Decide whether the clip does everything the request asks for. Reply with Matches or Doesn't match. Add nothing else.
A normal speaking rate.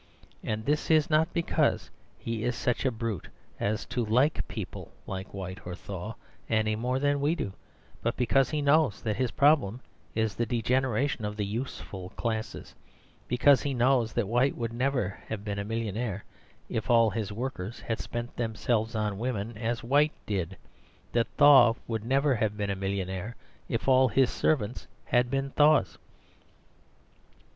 Matches